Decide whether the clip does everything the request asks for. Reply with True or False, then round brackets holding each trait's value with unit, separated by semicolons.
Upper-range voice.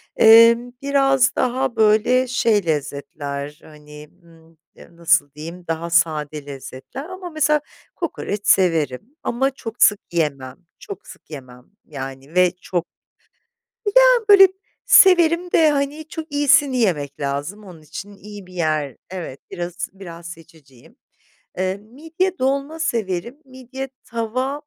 True (195 Hz)